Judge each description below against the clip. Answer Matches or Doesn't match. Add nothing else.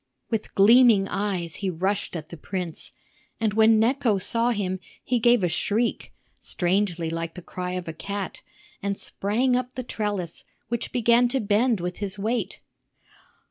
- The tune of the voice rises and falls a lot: Doesn't match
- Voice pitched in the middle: Doesn't match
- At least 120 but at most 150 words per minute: Doesn't match